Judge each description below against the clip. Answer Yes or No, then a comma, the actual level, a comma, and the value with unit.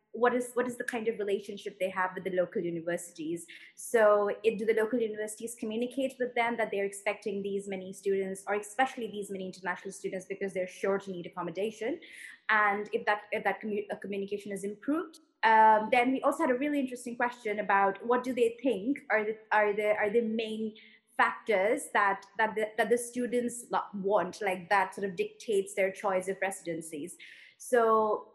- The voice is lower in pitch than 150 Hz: No, high, 215 Hz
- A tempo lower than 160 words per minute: No, average, 190 wpm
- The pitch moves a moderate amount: Yes, average, 3.2 semitones